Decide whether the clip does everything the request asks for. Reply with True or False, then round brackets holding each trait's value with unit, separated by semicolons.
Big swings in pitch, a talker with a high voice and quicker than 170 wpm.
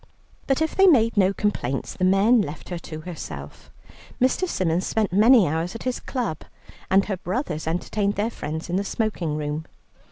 True (5.8 semitones; 195 Hz; 180 wpm)